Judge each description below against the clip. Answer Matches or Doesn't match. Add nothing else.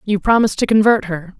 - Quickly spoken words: Matches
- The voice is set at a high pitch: Matches